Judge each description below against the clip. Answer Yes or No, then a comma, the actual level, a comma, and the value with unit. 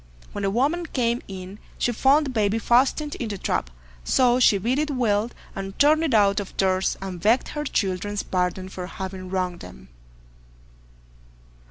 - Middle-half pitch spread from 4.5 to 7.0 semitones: Yes, average, 5.1 semitones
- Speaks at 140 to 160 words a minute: No, average, 170 wpm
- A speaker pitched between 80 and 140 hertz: No, high, 205 Hz